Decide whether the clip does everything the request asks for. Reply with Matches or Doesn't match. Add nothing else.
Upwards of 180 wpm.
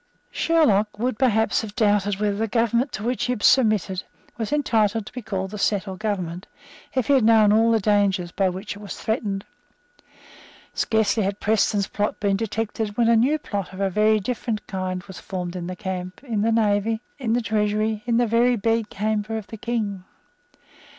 Matches